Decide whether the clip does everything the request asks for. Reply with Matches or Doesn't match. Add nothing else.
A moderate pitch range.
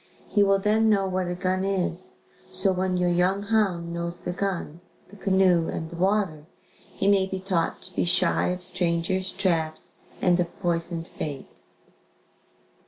Doesn't match